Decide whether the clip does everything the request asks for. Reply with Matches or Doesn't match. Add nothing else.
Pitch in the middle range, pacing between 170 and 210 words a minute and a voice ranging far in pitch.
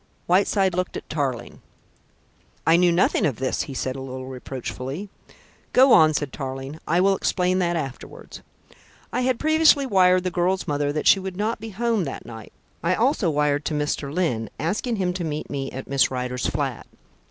Matches